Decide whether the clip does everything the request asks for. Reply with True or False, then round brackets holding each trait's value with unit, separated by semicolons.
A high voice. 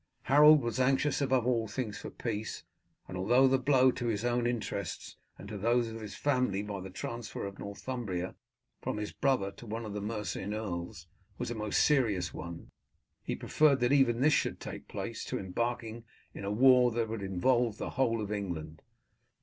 False (115 Hz)